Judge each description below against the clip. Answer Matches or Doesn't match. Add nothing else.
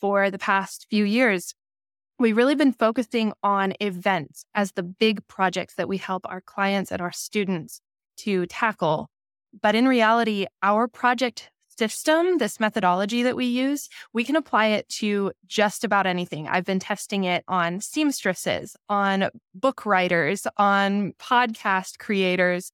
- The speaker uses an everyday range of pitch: Matches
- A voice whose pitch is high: Matches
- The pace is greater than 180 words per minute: Doesn't match